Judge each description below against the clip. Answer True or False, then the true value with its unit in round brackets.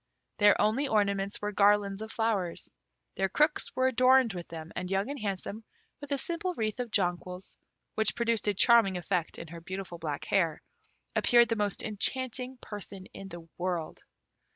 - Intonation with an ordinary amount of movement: True (4.3 semitones)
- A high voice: True (205 Hz)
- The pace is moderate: True (170 wpm)